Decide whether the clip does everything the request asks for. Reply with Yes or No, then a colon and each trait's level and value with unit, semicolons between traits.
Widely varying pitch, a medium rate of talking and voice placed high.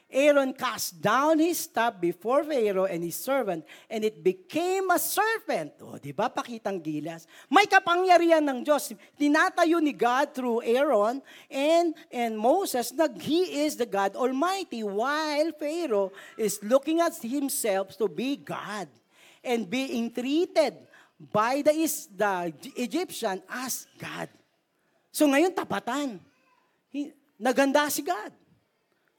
Yes: wide, 6.3 semitones; average, 130 wpm; very high, 275 Hz